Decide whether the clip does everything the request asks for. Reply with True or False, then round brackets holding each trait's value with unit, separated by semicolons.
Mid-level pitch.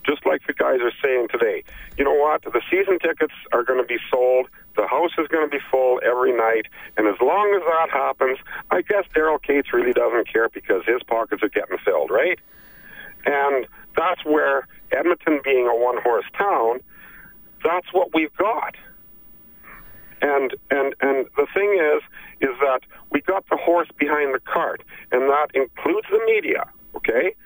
True (165 Hz)